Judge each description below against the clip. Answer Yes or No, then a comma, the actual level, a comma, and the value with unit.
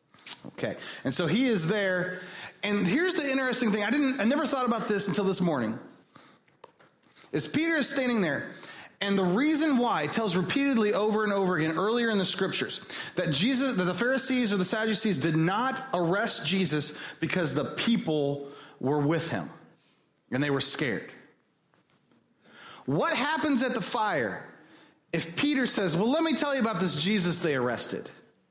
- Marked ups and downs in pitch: Yes, wide, 6.2 semitones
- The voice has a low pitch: No, high, 205 Hz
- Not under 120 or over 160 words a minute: No, average, 170 wpm